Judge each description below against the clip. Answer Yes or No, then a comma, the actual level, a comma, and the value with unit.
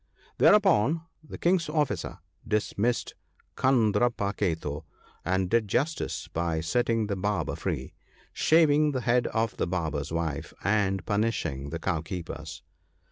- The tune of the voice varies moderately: No, wide, 6.6 semitones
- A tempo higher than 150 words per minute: No, slow, 135 wpm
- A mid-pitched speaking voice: No, low, 105 Hz